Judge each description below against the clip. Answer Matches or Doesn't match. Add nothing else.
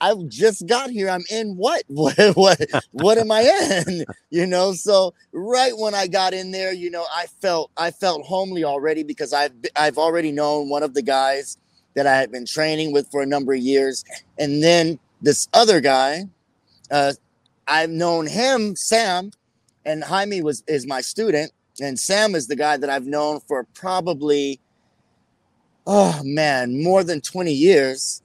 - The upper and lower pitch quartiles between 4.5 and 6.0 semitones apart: Matches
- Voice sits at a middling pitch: Matches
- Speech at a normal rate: Matches